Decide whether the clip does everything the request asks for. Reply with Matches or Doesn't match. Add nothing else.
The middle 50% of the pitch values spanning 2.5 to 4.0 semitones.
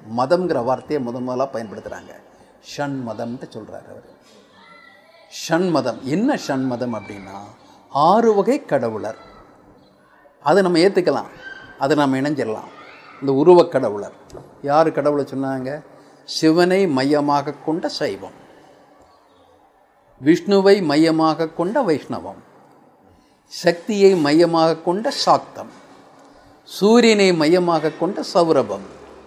Doesn't match